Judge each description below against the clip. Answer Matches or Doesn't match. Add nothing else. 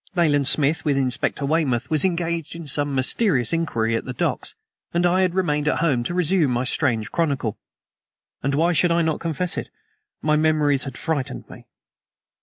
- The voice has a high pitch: Doesn't match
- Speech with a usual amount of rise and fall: Matches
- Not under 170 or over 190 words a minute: Matches